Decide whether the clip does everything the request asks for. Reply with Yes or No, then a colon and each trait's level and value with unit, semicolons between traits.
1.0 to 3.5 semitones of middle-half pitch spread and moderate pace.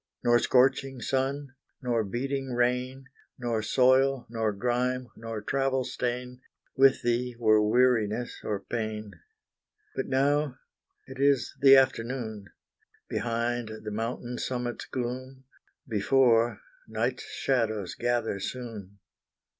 No: narrow, 2.5 semitones; slow, 105 wpm